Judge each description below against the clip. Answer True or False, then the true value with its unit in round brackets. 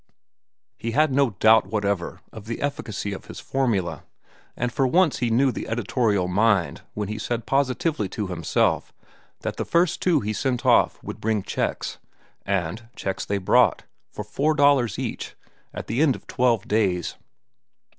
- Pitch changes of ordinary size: True (4.9 semitones)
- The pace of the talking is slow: False (165 wpm)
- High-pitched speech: False (115 Hz)